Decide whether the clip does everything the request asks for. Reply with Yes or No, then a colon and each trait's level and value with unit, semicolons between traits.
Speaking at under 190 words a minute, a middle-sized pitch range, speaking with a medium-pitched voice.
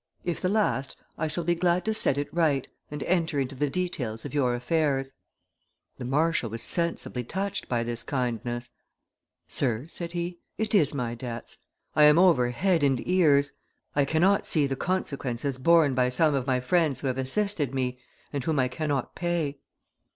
Yes: average, 180 wpm; average, 5.0 semitones; medium, 145 Hz